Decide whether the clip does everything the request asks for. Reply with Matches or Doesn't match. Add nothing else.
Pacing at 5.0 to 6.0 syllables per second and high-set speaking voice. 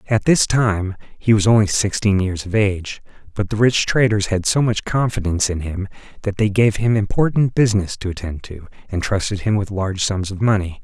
Doesn't match